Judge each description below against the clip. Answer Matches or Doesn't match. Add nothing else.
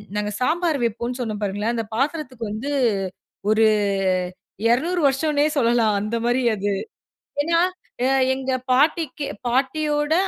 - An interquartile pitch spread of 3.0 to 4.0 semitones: Doesn't match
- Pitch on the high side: Matches